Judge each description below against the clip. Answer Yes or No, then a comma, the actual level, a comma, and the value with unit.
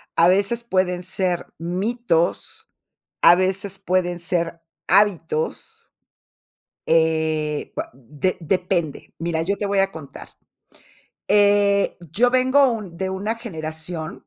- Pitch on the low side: No, medium, 185 Hz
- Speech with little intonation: No, average, 3.4 semitones